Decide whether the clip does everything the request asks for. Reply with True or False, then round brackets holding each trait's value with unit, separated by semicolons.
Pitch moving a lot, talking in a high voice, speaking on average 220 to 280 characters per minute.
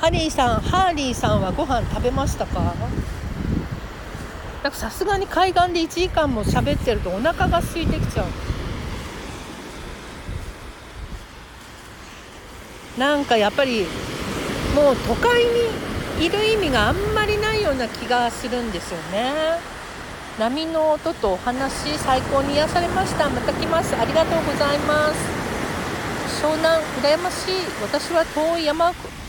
False (4.0 semitones; 315 Hz; 260 characters per minute)